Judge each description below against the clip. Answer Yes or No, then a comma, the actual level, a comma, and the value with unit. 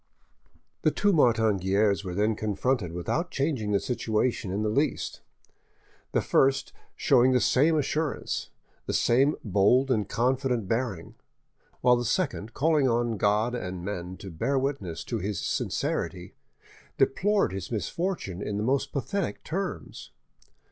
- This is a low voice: Yes, low, 115 Hz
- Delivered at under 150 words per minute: Yes, average, 140 wpm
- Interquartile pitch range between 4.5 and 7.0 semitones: Yes, average, 5.2 semitones